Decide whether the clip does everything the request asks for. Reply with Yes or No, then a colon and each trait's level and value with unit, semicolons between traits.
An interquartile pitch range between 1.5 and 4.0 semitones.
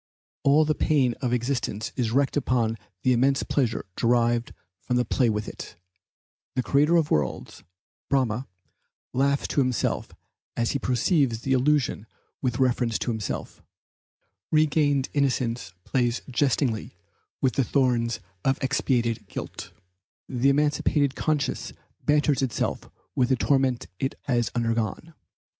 Yes: average, 2.9 semitones